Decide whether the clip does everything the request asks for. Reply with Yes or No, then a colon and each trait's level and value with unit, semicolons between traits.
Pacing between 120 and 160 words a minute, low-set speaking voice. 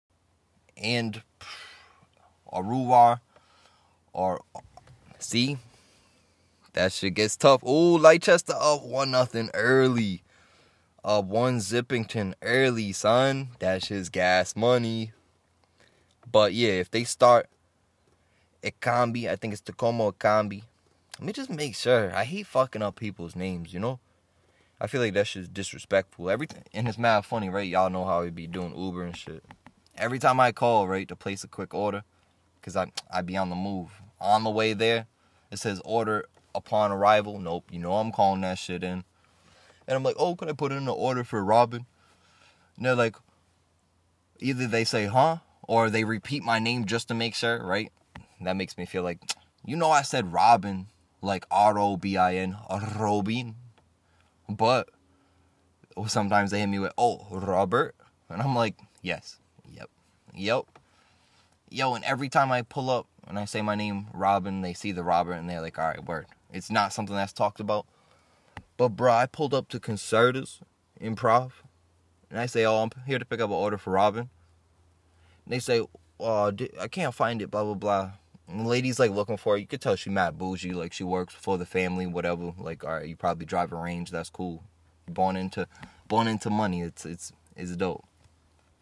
No: average, 180 wpm; low, 100 Hz